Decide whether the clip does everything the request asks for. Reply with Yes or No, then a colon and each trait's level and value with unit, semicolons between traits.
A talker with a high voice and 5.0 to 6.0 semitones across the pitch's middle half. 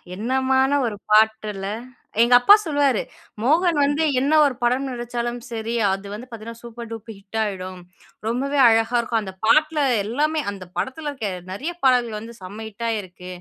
No: high, 235 Hz; average, 3.7 semitones